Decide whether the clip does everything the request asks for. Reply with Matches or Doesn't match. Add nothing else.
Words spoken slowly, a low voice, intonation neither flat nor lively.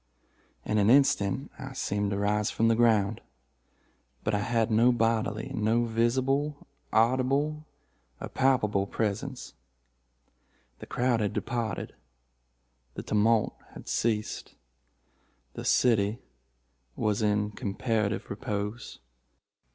Matches